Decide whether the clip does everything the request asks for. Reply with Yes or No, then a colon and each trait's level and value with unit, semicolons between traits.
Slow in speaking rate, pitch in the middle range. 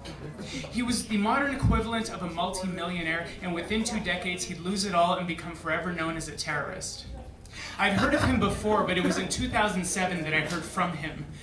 No: average, 200 wpm; medium, 180 Hz